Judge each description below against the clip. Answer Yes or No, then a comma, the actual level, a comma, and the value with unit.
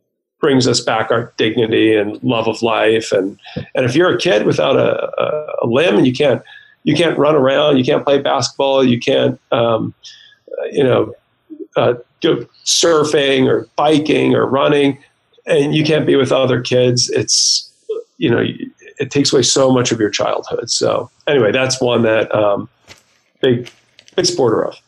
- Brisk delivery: No, average, 170 wpm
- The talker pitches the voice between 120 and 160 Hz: Yes, low, 135 Hz